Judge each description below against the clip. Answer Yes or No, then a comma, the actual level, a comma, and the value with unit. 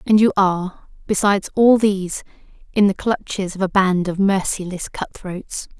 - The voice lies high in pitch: Yes, high, 195 Hz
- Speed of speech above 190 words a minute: No, average, 155 wpm